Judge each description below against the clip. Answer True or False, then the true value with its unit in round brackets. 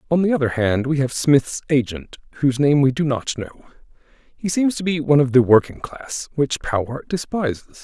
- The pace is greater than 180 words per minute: True (200 wpm)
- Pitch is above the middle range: False (140 Hz)